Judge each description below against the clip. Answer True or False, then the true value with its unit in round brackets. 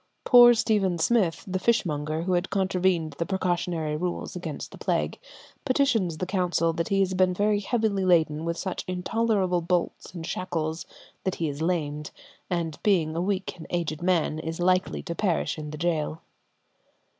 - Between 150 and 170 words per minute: True (165 wpm)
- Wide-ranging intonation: False (2.8 semitones)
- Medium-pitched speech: True (175 Hz)